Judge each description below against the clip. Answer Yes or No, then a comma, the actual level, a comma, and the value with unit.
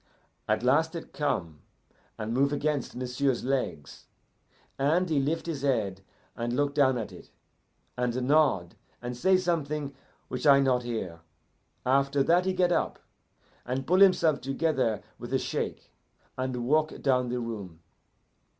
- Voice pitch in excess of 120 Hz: Yes, low, 135 Hz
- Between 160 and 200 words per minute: No, average, 145 wpm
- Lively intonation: No, average, 3.9 semitones